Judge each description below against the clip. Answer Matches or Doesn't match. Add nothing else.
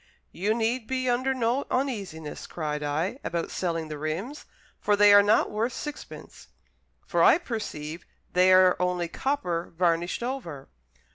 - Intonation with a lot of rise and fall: Matches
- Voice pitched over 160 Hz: Matches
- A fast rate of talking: Doesn't match